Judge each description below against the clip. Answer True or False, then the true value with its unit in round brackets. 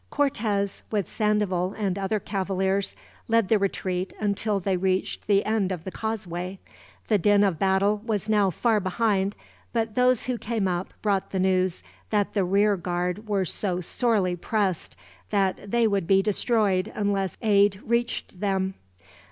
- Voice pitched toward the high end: True (200 Hz)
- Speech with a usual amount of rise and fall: False (2.1 semitones)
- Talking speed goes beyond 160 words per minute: False (155 wpm)